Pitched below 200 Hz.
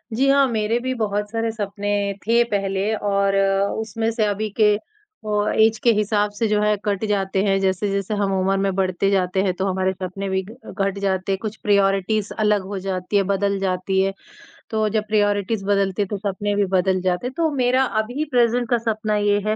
No: high, 205 Hz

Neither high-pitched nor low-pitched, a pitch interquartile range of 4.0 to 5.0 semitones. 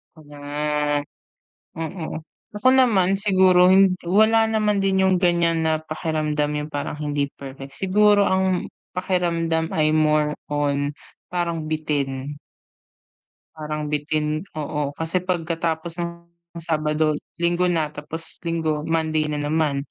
No: medium, 160 Hz; average, 3.3 semitones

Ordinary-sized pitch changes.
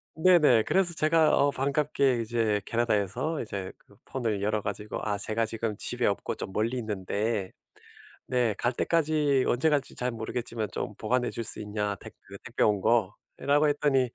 Yes: average, 4.8 semitones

